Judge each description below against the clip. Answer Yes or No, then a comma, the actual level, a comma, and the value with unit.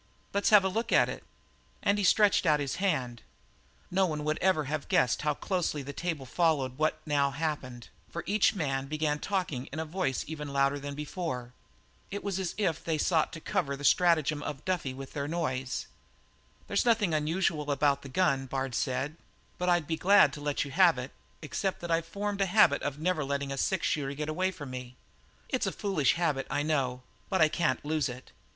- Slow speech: No, fast, 205 wpm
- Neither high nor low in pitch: Yes, medium, 155 Hz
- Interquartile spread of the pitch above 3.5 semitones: Yes, average, 4.5 semitones